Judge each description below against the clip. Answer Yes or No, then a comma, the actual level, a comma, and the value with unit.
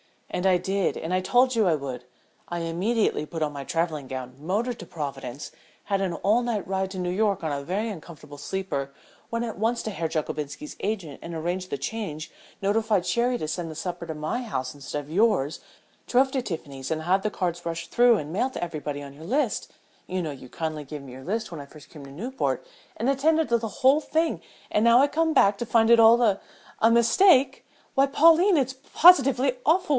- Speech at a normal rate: No, fast, 220 wpm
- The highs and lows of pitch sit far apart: Yes, wide, 7.3 semitones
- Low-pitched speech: No, high, 190 Hz